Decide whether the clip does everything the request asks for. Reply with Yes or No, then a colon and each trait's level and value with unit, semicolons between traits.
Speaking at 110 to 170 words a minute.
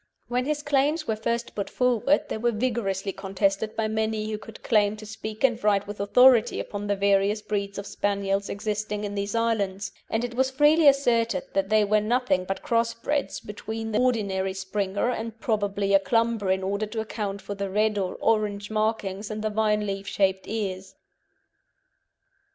No: average, 180 wpm